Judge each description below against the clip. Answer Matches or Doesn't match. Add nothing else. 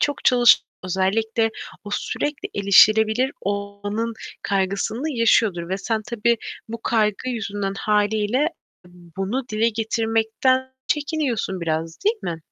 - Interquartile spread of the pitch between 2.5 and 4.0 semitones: Matches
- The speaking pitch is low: Doesn't match